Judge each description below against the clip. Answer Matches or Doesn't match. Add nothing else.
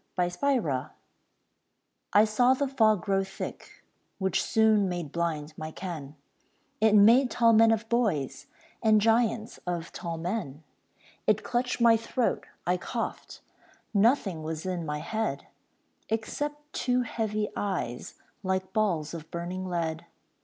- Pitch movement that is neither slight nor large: Matches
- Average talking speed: Doesn't match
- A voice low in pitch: Doesn't match